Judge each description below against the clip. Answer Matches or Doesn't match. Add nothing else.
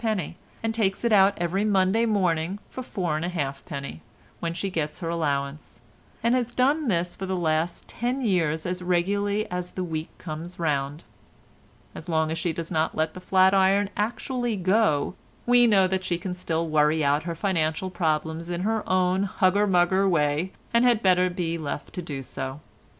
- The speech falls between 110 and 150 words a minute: Doesn't match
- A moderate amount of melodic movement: Matches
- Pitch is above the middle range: Doesn't match